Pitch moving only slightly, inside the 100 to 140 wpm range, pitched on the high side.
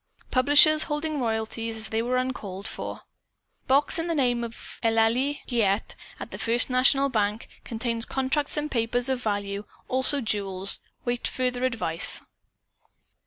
No: average, 3.2 semitones; slow, 135 wpm; high, 245 Hz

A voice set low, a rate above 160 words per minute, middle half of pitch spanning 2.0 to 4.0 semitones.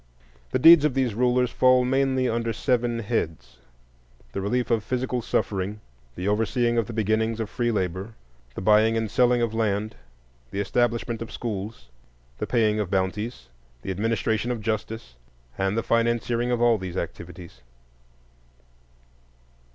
No: low, 115 Hz; average, 145 wpm; average, 2.8 semitones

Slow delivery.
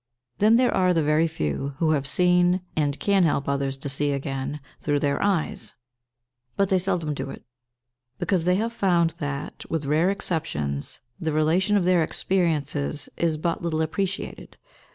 No: average, 165 wpm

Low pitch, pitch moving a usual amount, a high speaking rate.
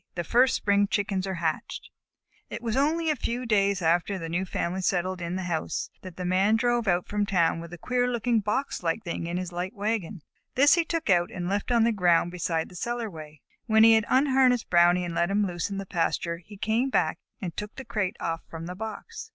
No: high, 195 Hz; average, 4.6 semitones; fast, 225 wpm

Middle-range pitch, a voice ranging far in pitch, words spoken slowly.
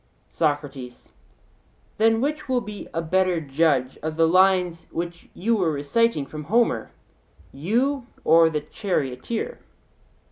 Yes: medium, 170 Hz; wide, 6.7 semitones; slow, 120 wpm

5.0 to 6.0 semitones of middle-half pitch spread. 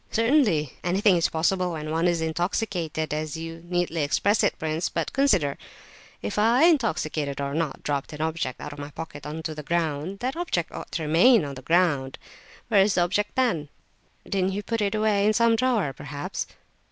Yes: average, 5.3 semitones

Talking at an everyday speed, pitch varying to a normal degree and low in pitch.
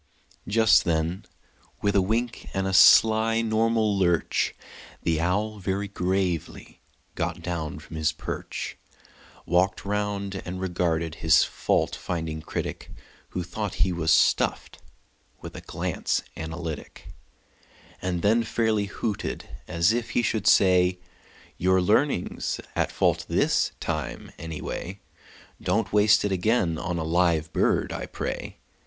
No: slow, 130 wpm; average, 3.8 semitones; very low, 95 Hz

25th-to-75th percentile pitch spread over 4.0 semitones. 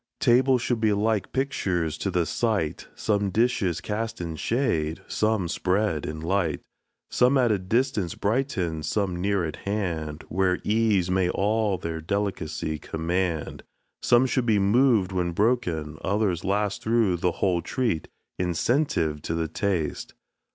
Yes: average, 4.6 semitones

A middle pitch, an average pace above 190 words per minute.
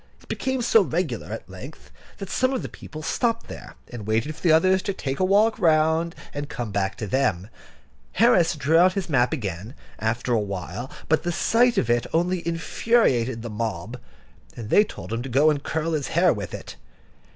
Yes: medium, 155 Hz; average, 200 wpm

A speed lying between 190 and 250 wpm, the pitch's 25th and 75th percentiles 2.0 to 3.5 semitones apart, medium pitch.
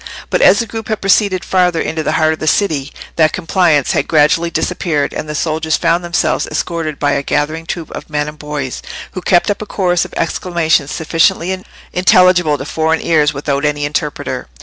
Yes: average, 195 wpm; average, 3.0 semitones; medium, 160 Hz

